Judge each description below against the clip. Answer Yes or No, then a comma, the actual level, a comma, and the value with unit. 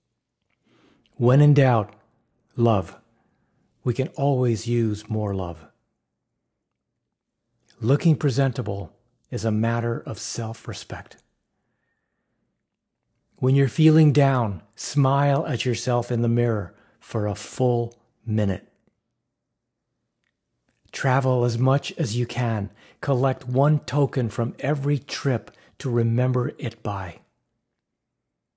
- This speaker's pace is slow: Yes, slow, 100 wpm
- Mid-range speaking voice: No, low, 120 Hz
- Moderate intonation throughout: Yes, average, 3.3 semitones